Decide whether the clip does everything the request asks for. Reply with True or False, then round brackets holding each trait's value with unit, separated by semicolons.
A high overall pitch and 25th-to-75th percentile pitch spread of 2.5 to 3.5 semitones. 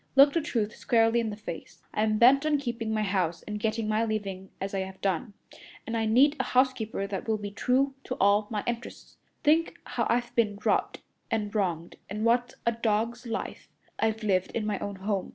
True (220 Hz; 2.8 semitones)